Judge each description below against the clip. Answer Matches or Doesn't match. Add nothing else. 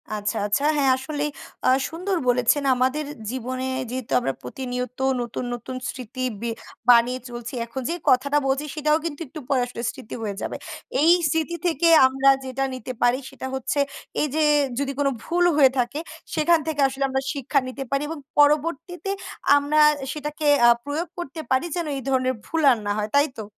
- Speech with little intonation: Doesn't match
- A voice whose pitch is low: Doesn't match